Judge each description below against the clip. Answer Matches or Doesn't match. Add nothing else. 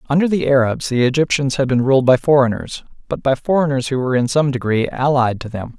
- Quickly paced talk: Matches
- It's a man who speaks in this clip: Matches